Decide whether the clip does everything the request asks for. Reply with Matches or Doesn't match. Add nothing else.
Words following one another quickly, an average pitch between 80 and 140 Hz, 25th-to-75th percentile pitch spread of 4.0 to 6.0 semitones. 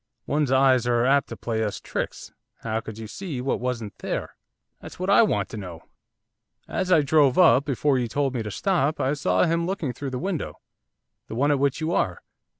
Matches